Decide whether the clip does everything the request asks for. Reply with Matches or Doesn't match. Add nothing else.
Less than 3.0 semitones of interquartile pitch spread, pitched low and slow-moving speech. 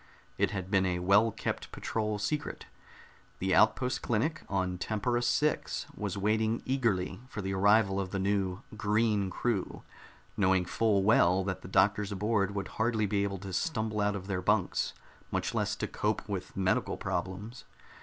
Doesn't match